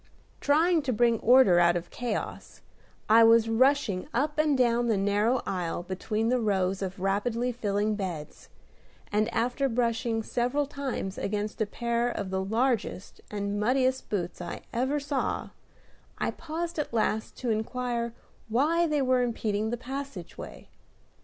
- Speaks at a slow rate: No, average, 145 wpm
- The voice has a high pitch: Yes, high, 230 Hz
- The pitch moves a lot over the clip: No, average, 3.9 semitones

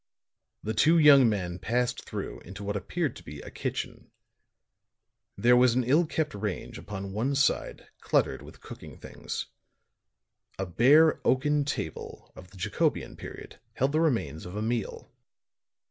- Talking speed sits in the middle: Yes, average, 150 wpm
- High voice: No, low, 120 Hz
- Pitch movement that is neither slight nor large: No, wide, 6.3 semitones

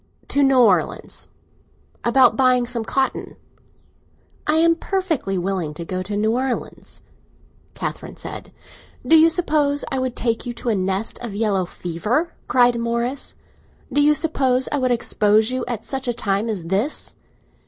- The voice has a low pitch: No, high, 240 Hz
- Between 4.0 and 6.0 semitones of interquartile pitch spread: Yes, average, 4.5 semitones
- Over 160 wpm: No, average, 155 wpm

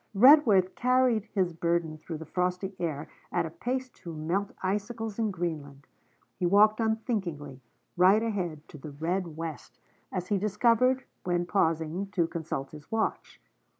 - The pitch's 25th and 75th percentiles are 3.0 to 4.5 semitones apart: No, average, 4.9 semitones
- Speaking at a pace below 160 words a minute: Yes, average, 150 wpm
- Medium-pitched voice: Yes, medium, 180 Hz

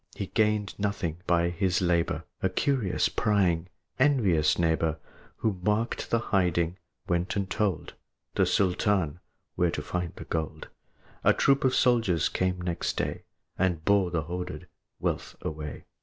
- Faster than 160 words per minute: No, average, 145 wpm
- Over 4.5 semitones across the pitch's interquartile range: No, average, 3.3 semitones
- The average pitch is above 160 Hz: No, very low, 90 Hz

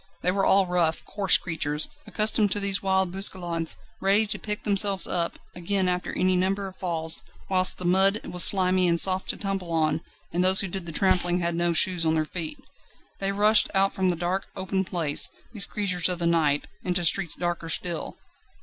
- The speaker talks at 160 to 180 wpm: No, average, 195 wpm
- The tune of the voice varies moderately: No, narrow, 2.2 semitones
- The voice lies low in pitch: No, medium, 185 Hz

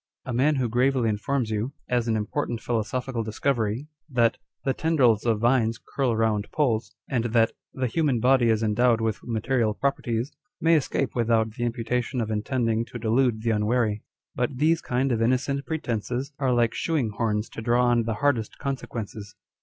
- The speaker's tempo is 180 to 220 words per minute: Yes, average, 185 wpm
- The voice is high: No, low, 120 Hz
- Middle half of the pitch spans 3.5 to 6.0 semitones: No, average, 2.8 semitones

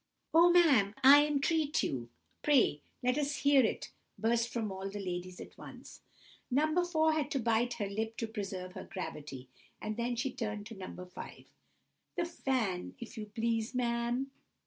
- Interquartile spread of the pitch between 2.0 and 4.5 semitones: No, wide, 5.5 semitones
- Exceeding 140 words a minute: Yes, average, 165 wpm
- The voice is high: Yes, high, 235 Hz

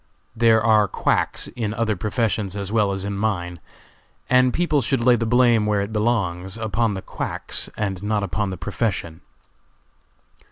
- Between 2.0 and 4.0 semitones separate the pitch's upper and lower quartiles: Yes, average, 2.8 semitones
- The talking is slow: No, average, 160 wpm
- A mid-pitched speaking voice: No, low, 105 Hz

